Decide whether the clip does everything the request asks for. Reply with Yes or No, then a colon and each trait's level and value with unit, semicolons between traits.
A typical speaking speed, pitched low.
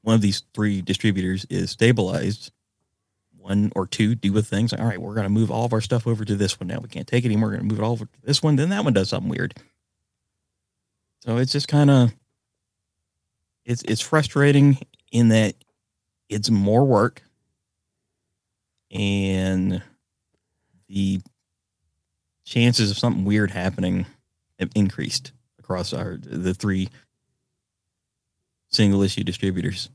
Yes: average, 155 wpm; low, 105 Hz